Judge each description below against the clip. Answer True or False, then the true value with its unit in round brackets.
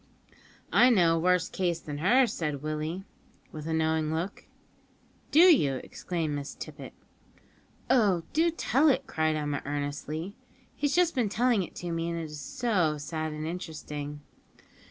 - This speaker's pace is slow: False (155 wpm)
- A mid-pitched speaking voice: True (165 Hz)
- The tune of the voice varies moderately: False (5.7 semitones)